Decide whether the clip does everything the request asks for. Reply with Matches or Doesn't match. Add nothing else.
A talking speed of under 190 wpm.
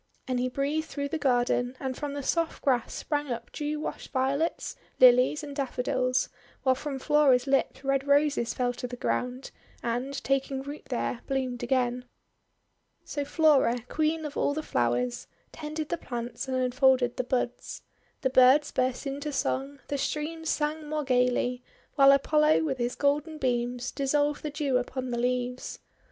Matches